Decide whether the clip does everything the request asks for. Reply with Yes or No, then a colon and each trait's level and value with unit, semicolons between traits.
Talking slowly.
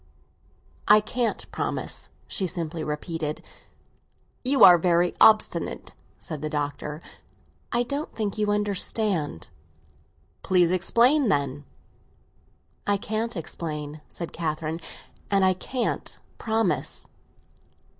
Yes: slow, 100 wpm